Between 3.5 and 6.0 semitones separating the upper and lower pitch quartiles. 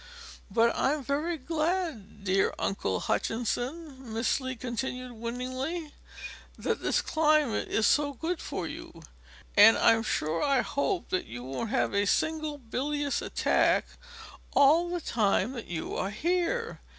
Yes: wide, 5.5 semitones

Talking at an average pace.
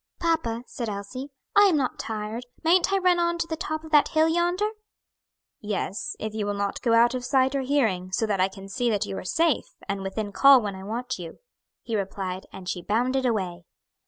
No: fast, 215 wpm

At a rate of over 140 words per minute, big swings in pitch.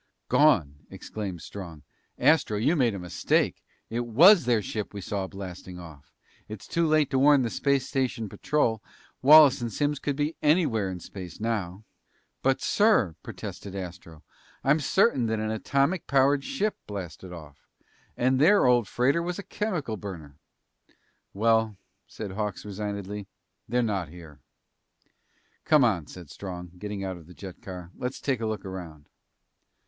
Yes: average, 155 wpm; wide, 6.8 semitones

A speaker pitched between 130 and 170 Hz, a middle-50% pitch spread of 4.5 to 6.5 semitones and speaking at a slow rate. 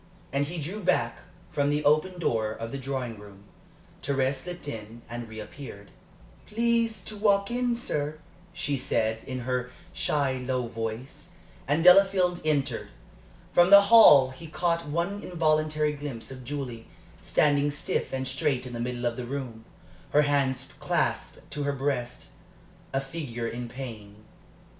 No: medium, 140 Hz; average, 5.0 semitones; average, 150 wpm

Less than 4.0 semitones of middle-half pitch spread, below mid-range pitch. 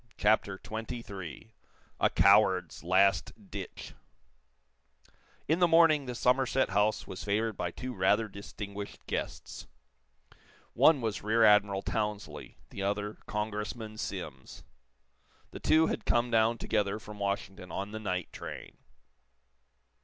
Yes: narrow, 2.4 semitones; low, 105 Hz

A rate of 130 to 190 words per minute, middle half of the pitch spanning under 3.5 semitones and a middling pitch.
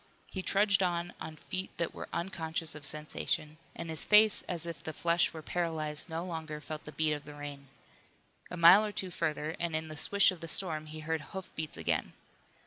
No: fast, 205 wpm; narrow, 2.4 semitones; medium, 160 Hz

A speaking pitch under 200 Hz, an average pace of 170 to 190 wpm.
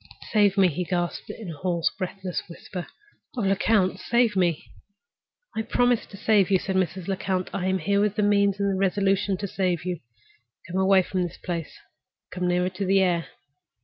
Yes: high, 190 Hz; average, 180 wpm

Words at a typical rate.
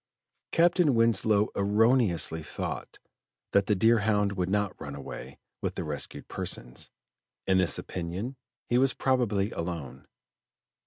No: slow, 120 wpm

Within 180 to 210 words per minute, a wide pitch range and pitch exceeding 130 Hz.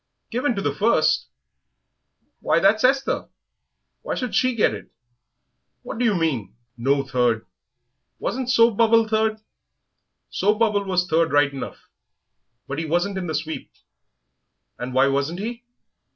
No: average, 145 wpm; wide, 7.7 semitones; high, 190 Hz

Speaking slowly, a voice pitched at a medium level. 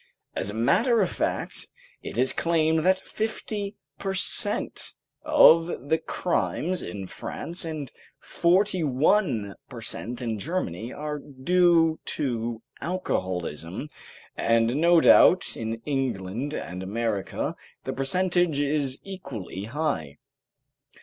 Yes: slow, 115 wpm; medium, 145 Hz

